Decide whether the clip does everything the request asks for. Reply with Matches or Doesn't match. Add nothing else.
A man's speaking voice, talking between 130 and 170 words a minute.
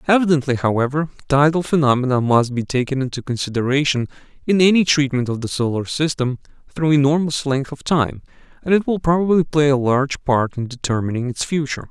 Matches